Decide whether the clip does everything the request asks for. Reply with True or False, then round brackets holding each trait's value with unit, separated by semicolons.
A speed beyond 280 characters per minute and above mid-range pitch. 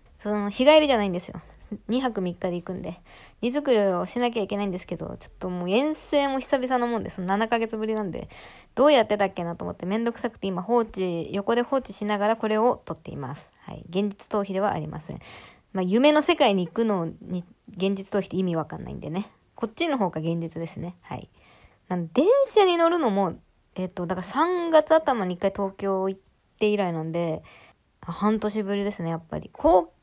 True (390 characters per minute; 205 Hz)